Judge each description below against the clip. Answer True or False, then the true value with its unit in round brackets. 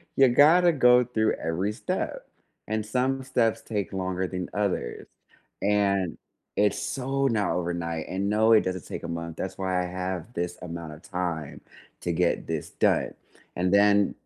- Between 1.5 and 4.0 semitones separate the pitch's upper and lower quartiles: False (4.4 semitones)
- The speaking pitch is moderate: False (100 Hz)